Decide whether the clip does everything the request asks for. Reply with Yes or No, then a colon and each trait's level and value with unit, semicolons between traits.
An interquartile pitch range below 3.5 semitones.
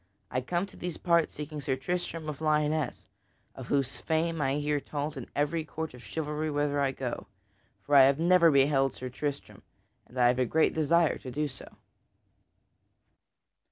Yes: average, 2.8 semitones